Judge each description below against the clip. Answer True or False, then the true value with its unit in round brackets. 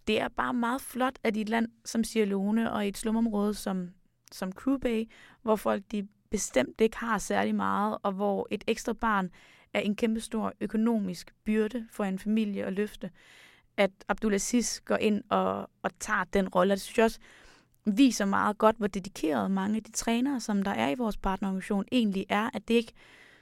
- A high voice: True (215 Hz)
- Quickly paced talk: False (190 wpm)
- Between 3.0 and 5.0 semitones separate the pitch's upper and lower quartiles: False (2.5 semitones)